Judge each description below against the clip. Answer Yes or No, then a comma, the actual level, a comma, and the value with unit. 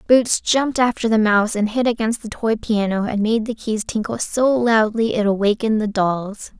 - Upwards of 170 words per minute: Yes, average, 200 wpm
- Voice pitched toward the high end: Yes, high, 220 Hz